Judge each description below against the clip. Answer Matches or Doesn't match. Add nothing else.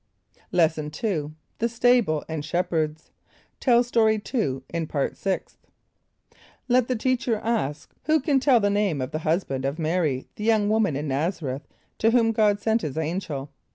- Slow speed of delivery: Doesn't match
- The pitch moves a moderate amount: Doesn't match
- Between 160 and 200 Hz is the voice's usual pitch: Matches